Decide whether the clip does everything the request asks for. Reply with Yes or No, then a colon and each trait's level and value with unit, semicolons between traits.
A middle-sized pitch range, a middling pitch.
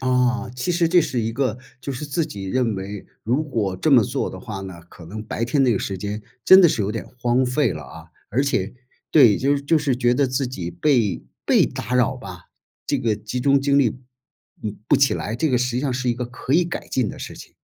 No: average, 4.5 semitones; low, 125 Hz